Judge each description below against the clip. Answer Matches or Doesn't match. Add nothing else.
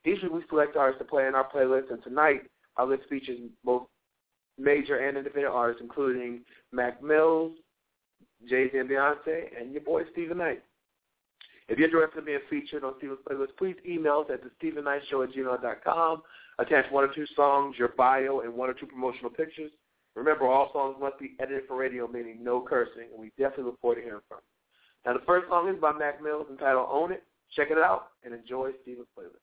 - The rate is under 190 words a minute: Doesn't match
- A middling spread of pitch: Matches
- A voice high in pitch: Doesn't match